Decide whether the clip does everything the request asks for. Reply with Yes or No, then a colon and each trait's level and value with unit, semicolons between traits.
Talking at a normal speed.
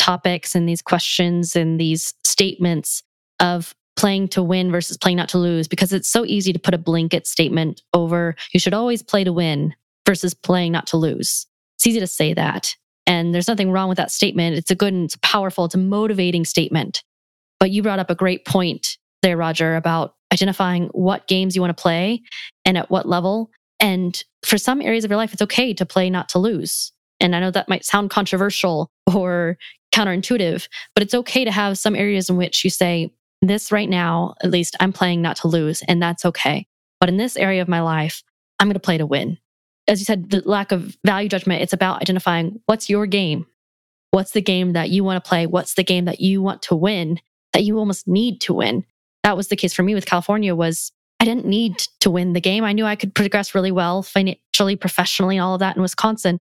No: fast, 220 wpm